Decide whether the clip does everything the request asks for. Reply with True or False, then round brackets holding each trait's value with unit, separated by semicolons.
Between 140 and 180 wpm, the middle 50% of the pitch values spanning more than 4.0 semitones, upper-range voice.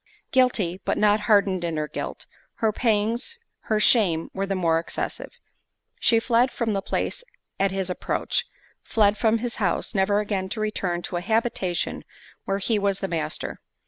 False (170 wpm; 3.0 semitones; 205 Hz)